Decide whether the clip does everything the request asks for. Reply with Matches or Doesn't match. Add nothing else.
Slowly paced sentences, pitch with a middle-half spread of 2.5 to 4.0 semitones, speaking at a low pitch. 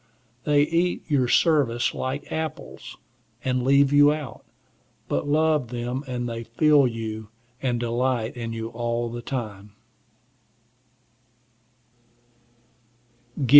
Matches